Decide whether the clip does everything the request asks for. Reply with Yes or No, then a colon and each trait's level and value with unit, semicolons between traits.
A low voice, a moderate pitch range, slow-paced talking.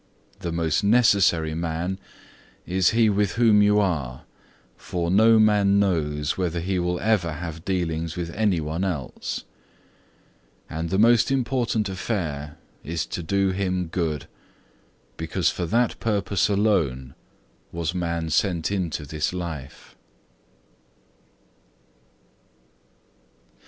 Yes: very low, 90 Hz; average, 3.8 semitones; slow, 115 wpm